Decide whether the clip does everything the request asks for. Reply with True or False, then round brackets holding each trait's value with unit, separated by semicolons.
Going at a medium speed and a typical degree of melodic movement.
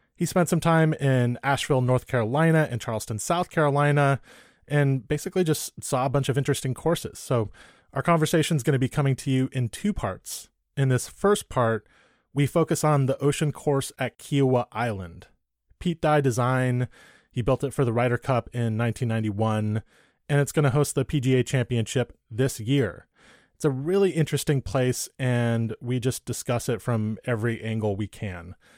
True (175 wpm; 3.7 semitones)